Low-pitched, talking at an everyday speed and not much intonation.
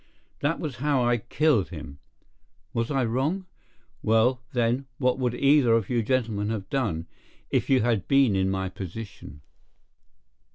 No: low, 120 Hz; average, 150 wpm; average, 4.4 semitones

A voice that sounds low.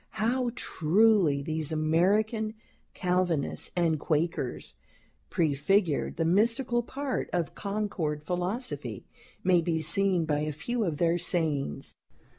No: medium, 175 Hz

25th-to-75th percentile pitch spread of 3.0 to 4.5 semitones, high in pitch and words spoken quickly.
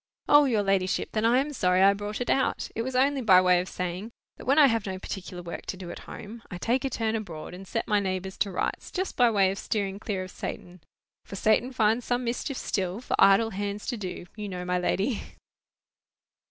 Yes: average, 4.0 semitones; high, 205 Hz; fast, 230 wpm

